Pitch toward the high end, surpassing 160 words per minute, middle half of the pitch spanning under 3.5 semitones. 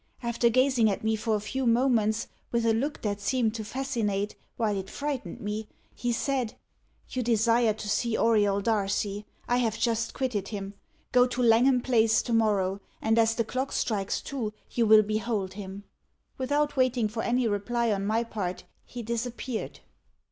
Yes: high, 225 Hz; average, 170 wpm; narrow, 2.6 semitones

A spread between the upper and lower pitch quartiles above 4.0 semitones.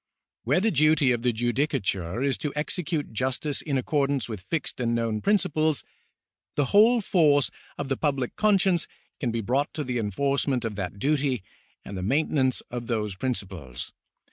Yes: average, 4.7 semitones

